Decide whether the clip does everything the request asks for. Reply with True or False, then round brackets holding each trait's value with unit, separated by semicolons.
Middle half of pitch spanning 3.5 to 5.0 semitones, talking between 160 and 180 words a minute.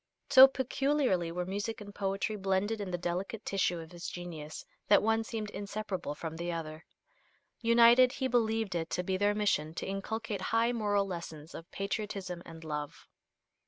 True (4.3 semitones; 165 wpm)